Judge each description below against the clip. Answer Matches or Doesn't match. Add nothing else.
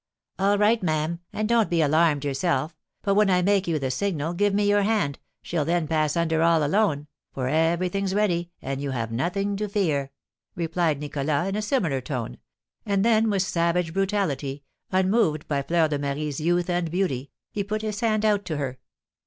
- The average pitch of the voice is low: Doesn't match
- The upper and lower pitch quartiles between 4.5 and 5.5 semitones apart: Matches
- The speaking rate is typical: Matches